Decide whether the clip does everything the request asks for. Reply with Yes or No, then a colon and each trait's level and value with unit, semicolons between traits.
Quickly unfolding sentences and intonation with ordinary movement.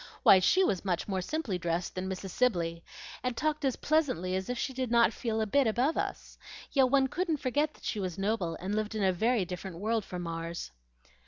No: fast, 220 wpm; wide, 5.9 semitones